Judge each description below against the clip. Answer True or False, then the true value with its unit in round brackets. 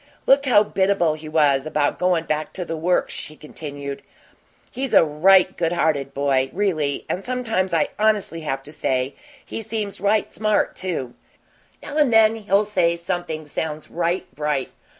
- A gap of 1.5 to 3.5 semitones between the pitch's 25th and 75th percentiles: False (5.2 semitones)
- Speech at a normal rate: True (165 wpm)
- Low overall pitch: False (170 Hz)